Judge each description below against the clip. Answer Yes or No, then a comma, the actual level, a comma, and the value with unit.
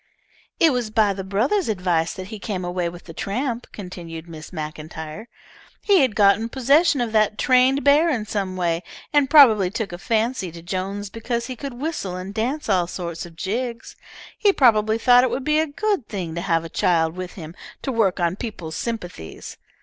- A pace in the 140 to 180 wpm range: No, average, 190 wpm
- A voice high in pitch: Yes, high, 210 Hz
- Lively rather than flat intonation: Yes, wide, 5.9 semitones